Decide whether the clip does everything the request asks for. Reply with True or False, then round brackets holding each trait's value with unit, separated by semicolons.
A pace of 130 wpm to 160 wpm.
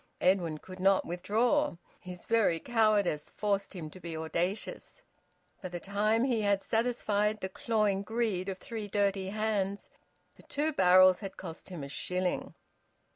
True (150 wpm)